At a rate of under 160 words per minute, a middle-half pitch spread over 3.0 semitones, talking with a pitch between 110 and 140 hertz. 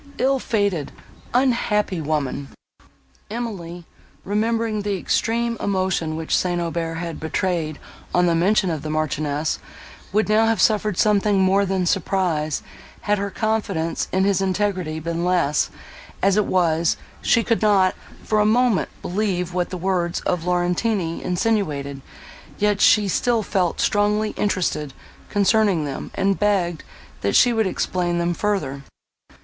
No: average, 140 wpm; average, 3.8 semitones; medium, 185 Hz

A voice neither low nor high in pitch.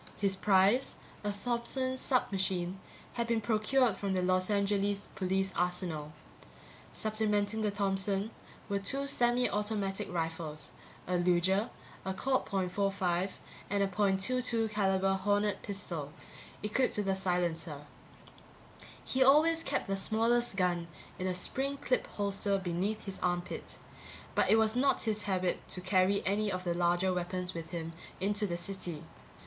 No: high, 195 Hz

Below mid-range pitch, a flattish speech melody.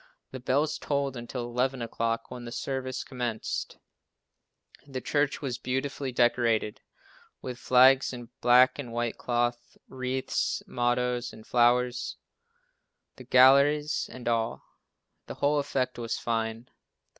Yes: low, 125 Hz; narrow, 1.8 semitones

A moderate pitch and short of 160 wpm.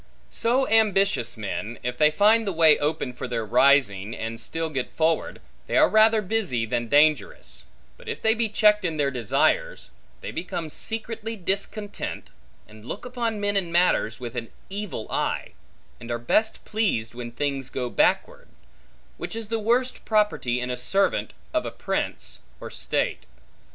No: medium, 160 Hz; average, 165 wpm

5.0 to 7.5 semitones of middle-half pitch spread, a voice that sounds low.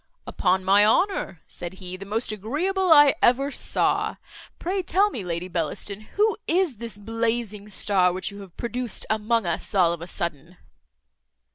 No: wide, 5.5 semitones; high, 210 Hz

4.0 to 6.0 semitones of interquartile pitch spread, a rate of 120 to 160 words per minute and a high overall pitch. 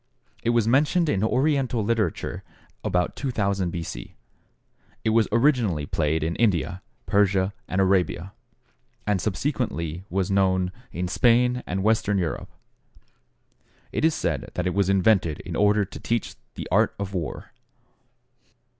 No: average, 4.3 semitones; slow, 135 wpm; low, 100 Hz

